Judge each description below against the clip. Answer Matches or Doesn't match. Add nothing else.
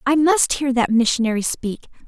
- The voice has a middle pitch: Doesn't match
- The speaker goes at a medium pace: Matches